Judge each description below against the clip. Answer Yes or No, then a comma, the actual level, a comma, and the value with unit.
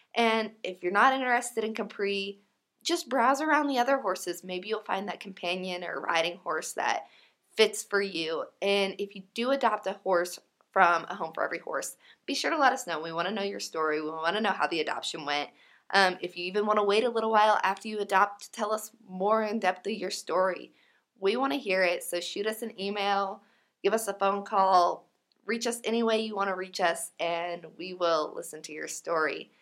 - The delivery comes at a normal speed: No, fast, 225 wpm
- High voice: Yes, high, 200 Hz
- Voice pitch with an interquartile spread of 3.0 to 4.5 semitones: Yes, average, 3.4 semitones